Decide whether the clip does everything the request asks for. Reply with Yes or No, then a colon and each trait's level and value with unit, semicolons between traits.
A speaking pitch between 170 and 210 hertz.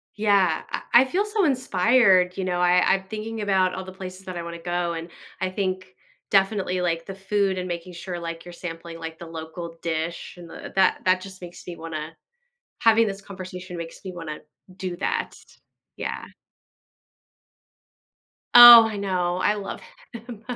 Yes: medium, 185 Hz